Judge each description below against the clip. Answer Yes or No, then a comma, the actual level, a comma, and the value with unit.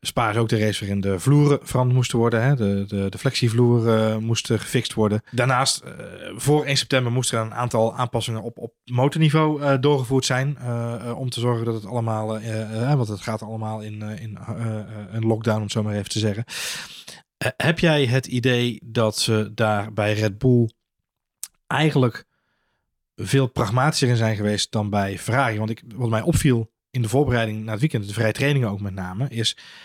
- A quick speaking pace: Yes, fast, 205 wpm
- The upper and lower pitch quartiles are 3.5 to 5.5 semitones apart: No, average, 3.0 semitones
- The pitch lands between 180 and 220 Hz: No, low, 115 Hz